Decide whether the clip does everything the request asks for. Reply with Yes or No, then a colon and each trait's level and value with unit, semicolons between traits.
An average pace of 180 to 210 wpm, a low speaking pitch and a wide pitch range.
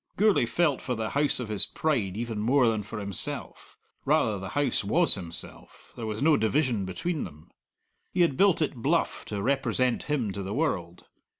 Yes: average, 185 wpm; low, 120 Hz; wide, 6.2 semitones